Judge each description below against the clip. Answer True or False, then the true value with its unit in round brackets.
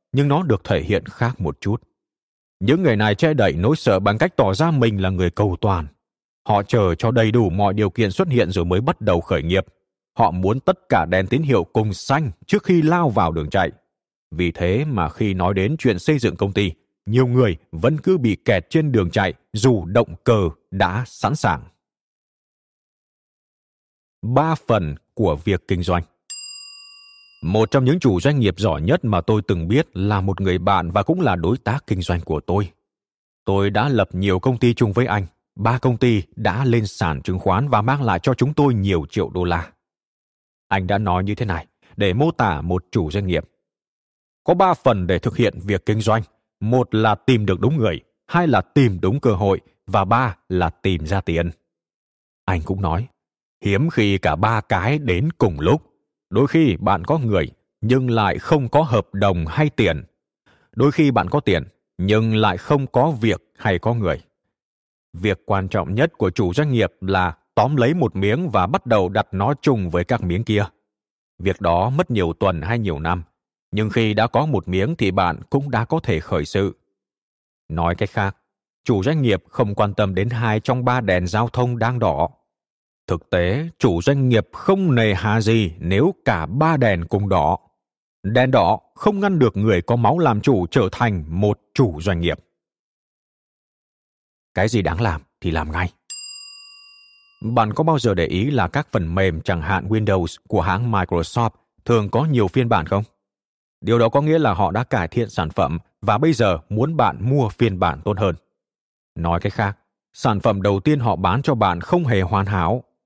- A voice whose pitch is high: False (105 Hz)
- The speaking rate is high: False (200 wpm)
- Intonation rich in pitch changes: False (5.0 semitones)